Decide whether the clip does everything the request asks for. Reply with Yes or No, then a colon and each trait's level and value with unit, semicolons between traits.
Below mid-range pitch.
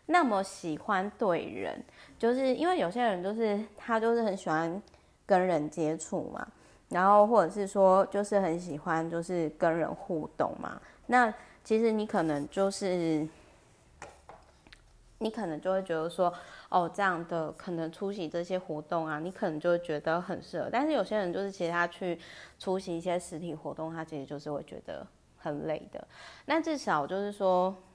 No: medium, 180 Hz